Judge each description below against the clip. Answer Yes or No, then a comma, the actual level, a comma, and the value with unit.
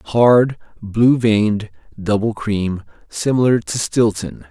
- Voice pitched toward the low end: Yes, low, 110 Hz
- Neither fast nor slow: No, slow, 105 wpm